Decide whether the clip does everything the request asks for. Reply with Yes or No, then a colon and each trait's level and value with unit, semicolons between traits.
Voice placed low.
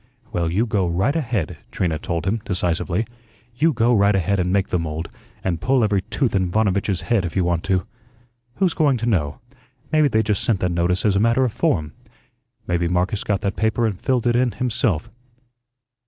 Yes: low, 100 Hz